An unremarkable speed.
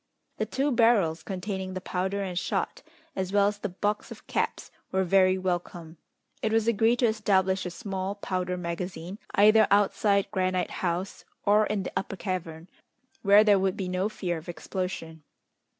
Yes: average, 165 wpm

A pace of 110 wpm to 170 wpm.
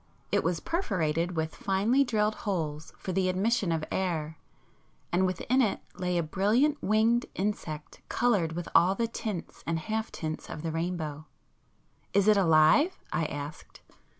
Yes: average, 150 wpm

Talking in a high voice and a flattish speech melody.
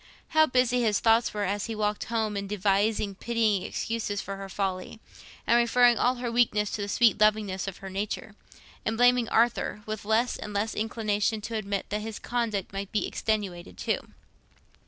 Yes: high, 215 Hz; narrow, 2.3 semitones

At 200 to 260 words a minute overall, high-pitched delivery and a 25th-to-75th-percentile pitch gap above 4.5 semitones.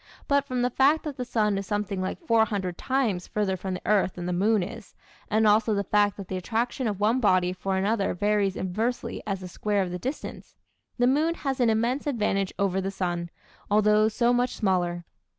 No: fast, 205 wpm; high, 210 Hz; average, 3.9 semitones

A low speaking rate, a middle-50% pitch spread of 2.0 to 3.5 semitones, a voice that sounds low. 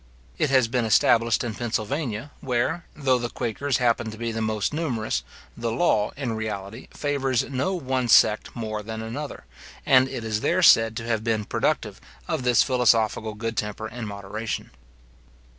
No: average, 165 wpm; average, 2.8 semitones; low, 115 Hz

